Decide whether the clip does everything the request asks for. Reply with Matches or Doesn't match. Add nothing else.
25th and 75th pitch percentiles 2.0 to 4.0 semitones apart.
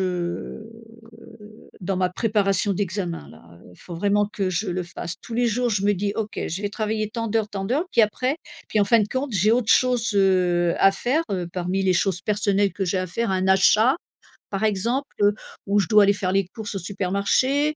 Matches